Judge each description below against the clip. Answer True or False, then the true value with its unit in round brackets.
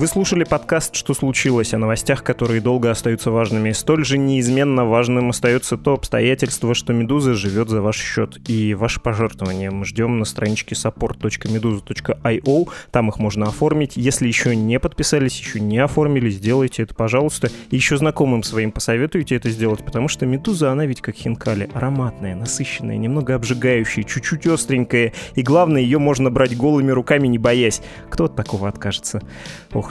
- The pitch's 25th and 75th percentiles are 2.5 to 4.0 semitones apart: True (3.5 semitones)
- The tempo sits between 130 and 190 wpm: True (160 wpm)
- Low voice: True (125 Hz)